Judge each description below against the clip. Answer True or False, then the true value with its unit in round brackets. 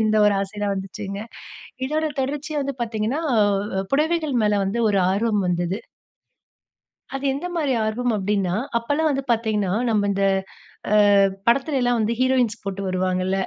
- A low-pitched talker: False (220 Hz)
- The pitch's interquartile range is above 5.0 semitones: True (5.4 semitones)